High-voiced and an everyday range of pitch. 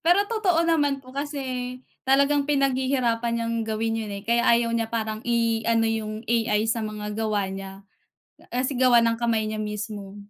Yes: high, 230 Hz; average, 3.3 semitones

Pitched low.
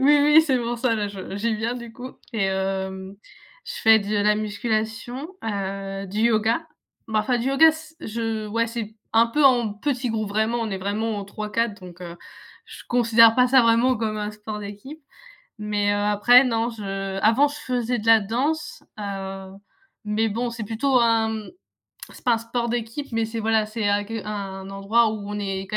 No: high, 220 Hz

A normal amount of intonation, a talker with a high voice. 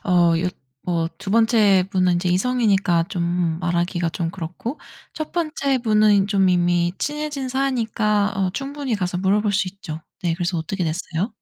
Yes: average, 4.3 semitones; high, 195 Hz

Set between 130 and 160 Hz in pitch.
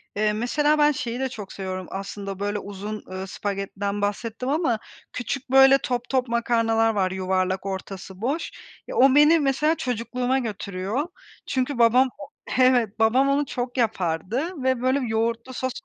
No: high, 235 Hz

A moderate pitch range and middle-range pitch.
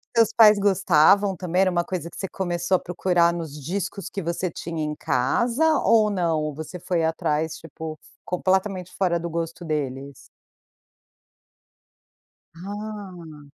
Yes: average, 3.2 semitones; medium, 175 Hz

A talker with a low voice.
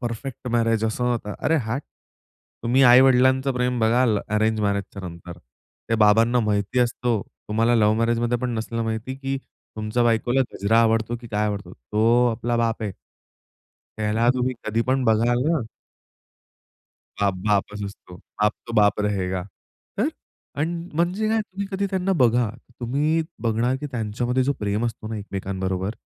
Yes: low, 115 Hz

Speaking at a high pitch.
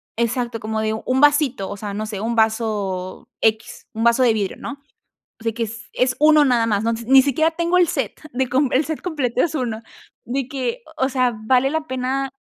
Yes: very high, 250 Hz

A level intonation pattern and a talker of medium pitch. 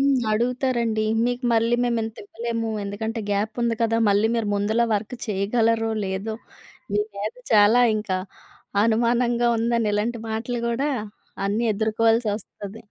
No: narrow, 1.9 semitones; high, 225 Hz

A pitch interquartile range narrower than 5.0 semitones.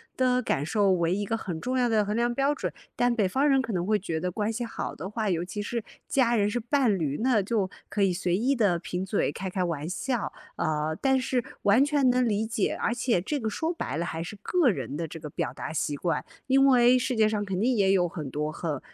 No: wide, 5.6 semitones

